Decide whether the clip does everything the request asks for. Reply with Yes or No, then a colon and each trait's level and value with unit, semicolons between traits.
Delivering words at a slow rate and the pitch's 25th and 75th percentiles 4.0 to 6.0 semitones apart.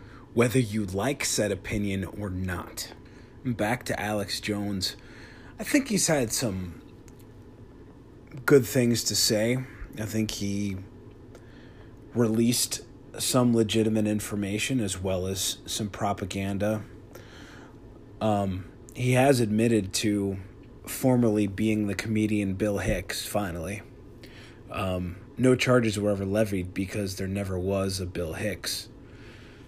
No: slow, 115 wpm; average, 3.3 semitones